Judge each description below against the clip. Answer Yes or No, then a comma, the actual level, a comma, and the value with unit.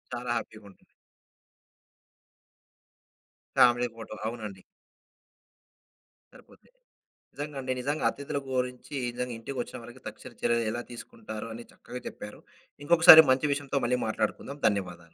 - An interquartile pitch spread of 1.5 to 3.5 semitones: No, average, 3.9 semitones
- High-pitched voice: No, low, 125 Hz